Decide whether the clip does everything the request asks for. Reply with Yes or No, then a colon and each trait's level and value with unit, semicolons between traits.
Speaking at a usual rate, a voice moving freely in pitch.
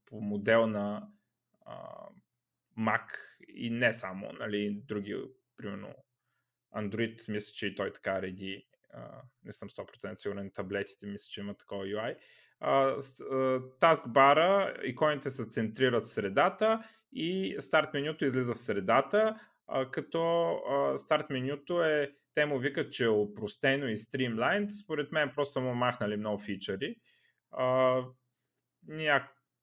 Yes: average, 125 wpm; wide, 5.7 semitones